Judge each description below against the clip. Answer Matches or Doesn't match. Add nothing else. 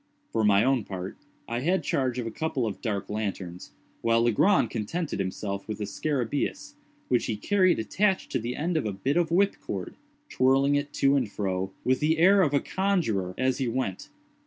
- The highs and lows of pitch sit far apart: Matches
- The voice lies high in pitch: Doesn't match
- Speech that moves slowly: Doesn't match